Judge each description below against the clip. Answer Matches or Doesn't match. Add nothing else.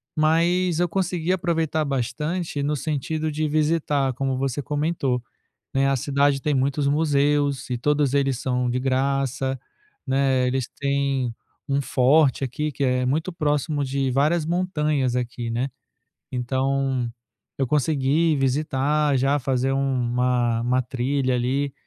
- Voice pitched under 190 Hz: Matches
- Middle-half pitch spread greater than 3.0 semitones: Doesn't match